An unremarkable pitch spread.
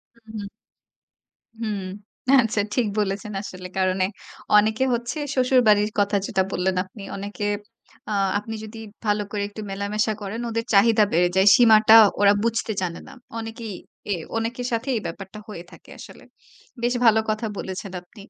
No: narrow, 2.2 semitones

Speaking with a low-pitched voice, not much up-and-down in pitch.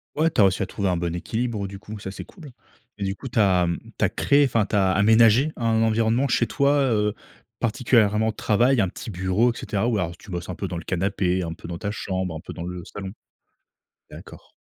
No: low, 105 Hz; average, 3.7 semitones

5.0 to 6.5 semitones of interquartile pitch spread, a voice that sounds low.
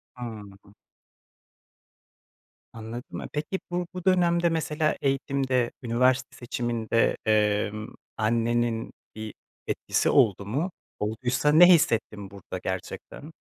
Yes: wide, 5.4 semitones; low, 120 Hz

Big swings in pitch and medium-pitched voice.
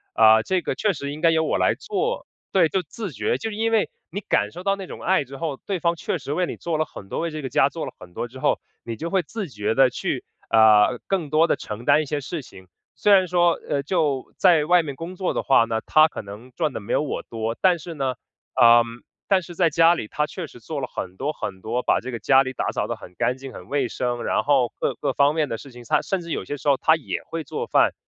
Yes: wide, 5.7 semitones; medium, 150 Hz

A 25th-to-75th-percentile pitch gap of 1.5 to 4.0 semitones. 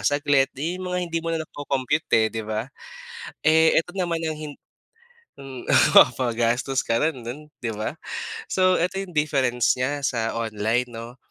No: average, 5.2 semitones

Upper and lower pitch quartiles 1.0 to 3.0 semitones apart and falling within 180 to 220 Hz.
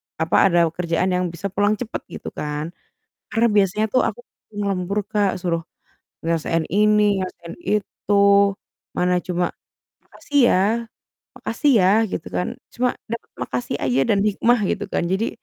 No: average, 3.7 semitones; high, 190 Hz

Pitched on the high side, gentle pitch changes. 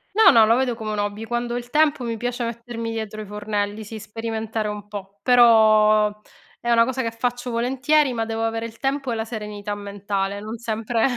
Yes: high, 225 Hz; narrow, 2.2 semitones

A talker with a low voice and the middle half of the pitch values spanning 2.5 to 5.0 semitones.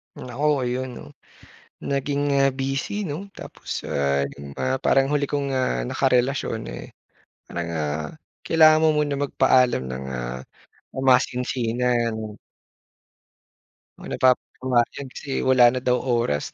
Yes: low, 125 Hz; average, 3.4 semitones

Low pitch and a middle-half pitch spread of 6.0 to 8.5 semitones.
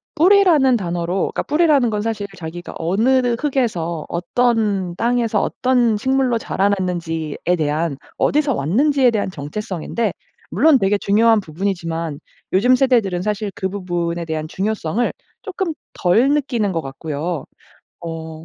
No: high, 200 Hz; wide, 6.4 semitones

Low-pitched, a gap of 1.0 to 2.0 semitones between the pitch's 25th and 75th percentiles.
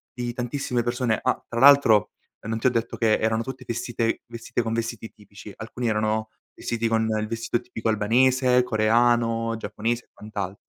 Yes: low, 115 Hz; narrow, 1.5 semitones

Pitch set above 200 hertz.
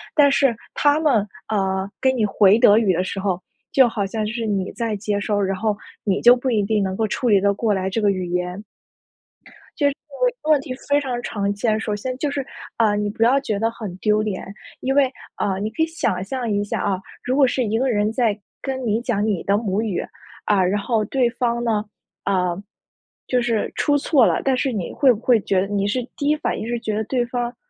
Yes: high, 220 Hz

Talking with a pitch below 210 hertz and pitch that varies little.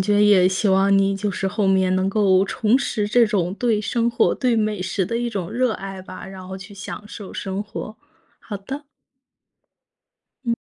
Yes: high, 200 Hz; narrow, 2.3 semitones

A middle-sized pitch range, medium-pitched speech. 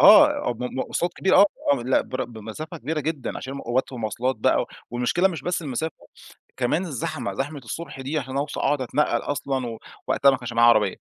No: average, 4.0 semitones; low, 130 Hz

